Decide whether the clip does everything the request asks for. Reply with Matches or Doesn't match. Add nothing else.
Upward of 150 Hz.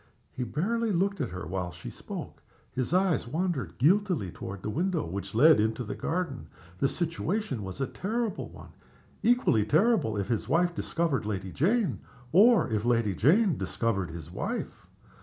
Doesn't match